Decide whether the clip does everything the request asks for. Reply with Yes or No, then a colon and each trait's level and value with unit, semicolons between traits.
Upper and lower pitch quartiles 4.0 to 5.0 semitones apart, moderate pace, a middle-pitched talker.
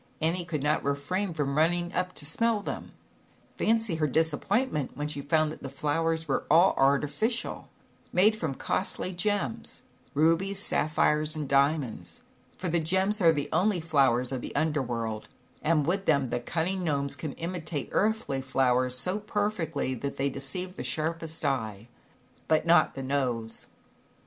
Yes: average, 4.4 semitones; average, 160 wpm; medium, 155 Hz